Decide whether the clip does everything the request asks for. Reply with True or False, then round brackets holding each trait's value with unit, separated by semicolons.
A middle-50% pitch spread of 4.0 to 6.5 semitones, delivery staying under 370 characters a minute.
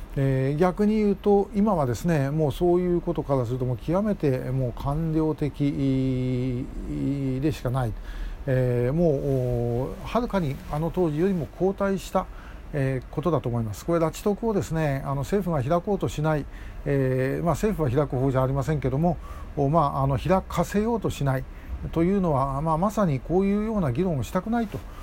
True (5.3 semitones; 330 characters per minute)